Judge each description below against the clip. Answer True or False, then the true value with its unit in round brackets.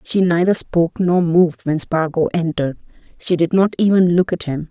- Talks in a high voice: False (170 Hz)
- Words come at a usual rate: True (190 wpm)